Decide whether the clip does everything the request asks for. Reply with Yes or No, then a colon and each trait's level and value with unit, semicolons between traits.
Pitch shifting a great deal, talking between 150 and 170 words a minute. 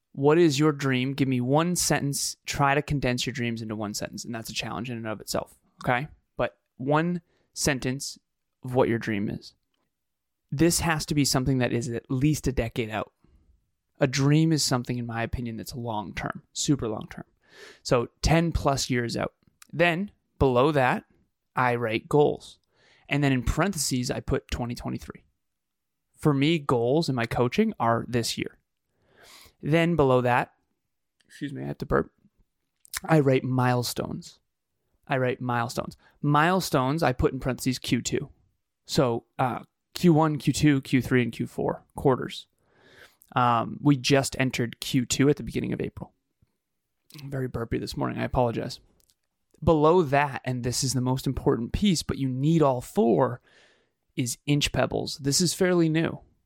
No: average, 3.8 semitones; average, 160 wpm